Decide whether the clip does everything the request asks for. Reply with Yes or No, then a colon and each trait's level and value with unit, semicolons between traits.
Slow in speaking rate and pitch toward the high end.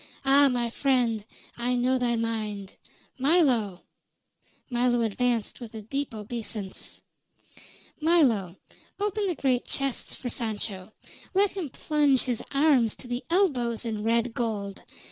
Yes: slow, 125 wpm; high, 245 Hz